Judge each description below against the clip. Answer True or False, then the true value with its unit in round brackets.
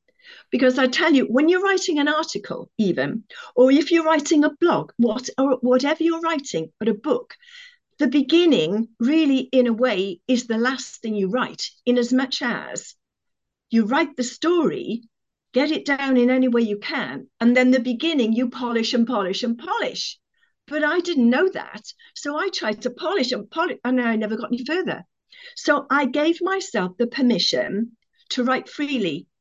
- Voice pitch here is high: True (260 Hz)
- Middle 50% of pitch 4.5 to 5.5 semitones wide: True (5.2 semitones)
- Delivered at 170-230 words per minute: True (180 wpm)